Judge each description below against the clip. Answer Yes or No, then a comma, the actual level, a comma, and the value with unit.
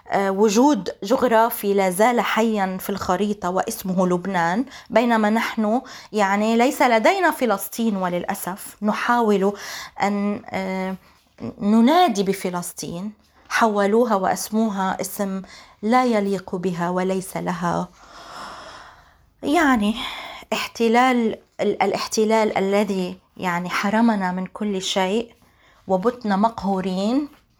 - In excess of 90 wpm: No, average, 85 wpm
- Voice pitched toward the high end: Yes, high, 205 Hz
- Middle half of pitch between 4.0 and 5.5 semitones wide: No, average, 3.3 semitones